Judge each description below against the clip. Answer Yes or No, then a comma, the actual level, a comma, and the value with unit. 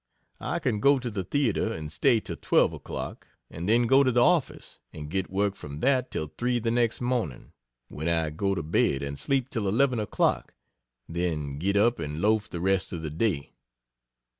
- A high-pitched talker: No, low, 100 Hz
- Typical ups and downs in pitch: No, wide, 7.1 semitones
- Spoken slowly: No, average, 195 wpm